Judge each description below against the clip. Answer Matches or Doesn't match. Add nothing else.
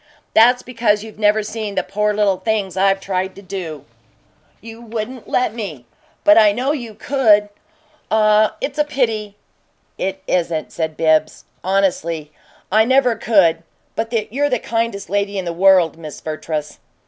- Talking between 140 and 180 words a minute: Matches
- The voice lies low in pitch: Doesn't match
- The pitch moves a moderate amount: Matches